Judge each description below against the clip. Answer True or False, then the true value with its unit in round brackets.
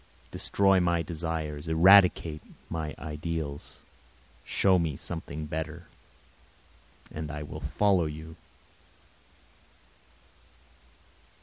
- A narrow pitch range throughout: True (2.1 semitones)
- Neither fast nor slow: False (80 wpm)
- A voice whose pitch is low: True (80 Hz)